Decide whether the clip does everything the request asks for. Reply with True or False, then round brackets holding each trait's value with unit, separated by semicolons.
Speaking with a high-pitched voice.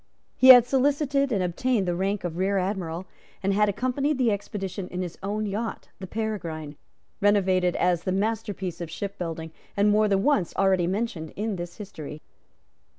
True (195 Hz)